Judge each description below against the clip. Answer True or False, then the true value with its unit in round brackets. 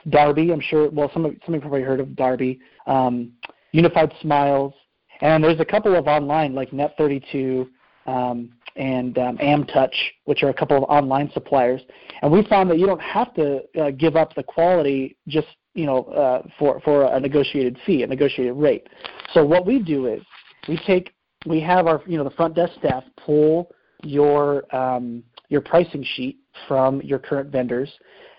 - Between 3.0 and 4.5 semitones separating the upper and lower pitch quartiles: True (3.3 semitones)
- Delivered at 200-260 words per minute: False (180 wpm)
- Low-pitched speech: False (145 Hz)